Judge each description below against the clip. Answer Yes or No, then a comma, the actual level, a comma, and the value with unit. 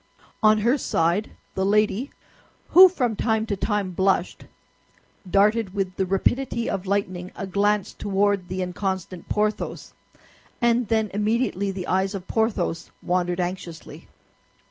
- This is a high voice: Yes, high, 200 Hz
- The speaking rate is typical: No, slow, 130 wpm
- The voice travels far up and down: No, narrow, 2.6 semitones